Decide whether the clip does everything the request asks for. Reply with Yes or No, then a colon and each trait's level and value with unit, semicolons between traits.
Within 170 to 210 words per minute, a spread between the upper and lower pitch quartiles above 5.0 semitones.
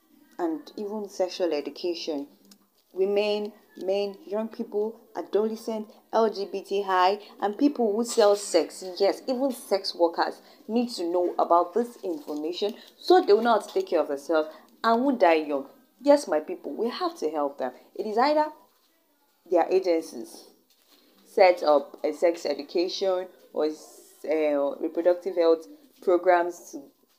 No: slow, 135 wpm; wide, 5.5 semitones